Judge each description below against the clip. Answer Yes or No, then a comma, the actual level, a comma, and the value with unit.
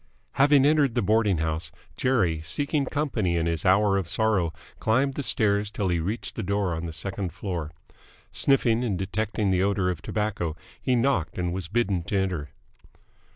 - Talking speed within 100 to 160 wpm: No, average, 175 wpm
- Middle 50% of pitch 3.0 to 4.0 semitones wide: No, average, 4.8 semitones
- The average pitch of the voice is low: Yes, low, 100 Hz